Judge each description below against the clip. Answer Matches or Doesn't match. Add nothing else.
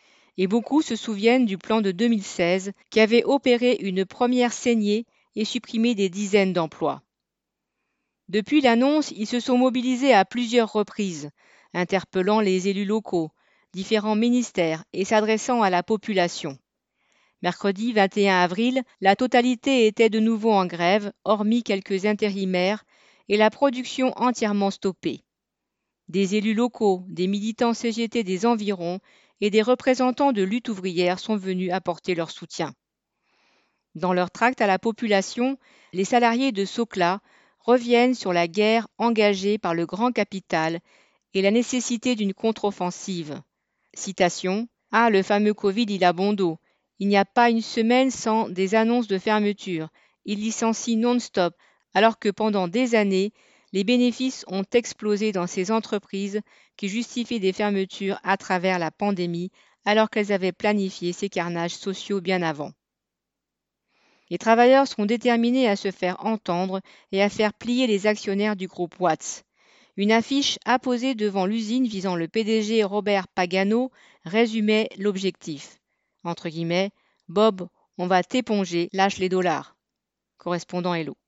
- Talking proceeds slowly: Matches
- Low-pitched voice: Doesn't match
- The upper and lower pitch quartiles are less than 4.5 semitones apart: Matches